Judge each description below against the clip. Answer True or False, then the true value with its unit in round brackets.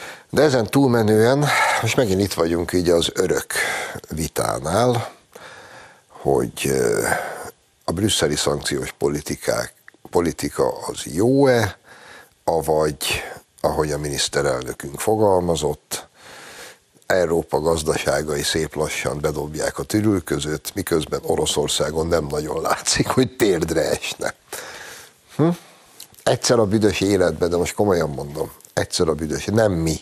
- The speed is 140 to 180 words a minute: False (105 wpm)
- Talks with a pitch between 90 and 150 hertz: True (105 Hz)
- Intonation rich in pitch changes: True (6.3 semitones)